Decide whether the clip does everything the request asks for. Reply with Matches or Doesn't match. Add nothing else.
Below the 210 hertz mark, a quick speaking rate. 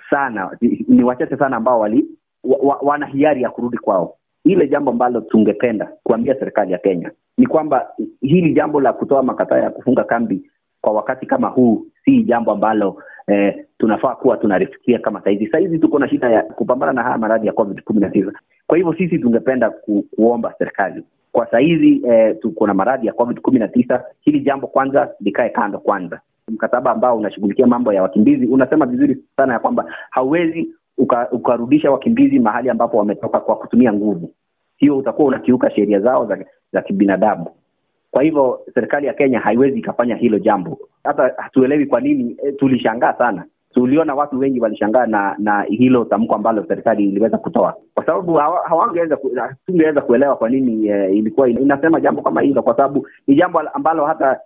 Matches